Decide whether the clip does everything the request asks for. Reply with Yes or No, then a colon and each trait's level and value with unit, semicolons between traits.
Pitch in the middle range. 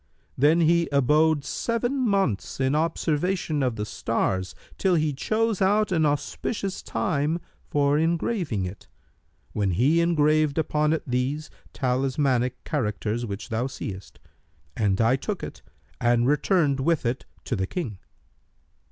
Yes: medium, 145 Hz